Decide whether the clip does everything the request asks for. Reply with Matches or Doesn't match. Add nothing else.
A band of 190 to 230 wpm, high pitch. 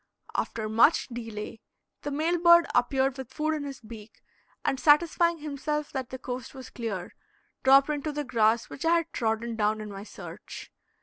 Doesn't match